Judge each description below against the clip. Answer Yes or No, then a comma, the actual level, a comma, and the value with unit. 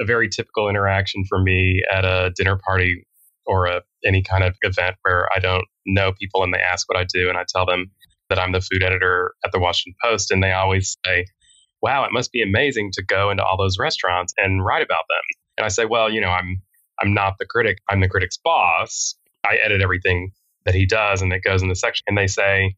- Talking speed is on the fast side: Yes, fast, 235 wpm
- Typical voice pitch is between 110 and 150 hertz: No, very low, 95 Hz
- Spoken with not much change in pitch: Yes, narrow, 1.4 semitones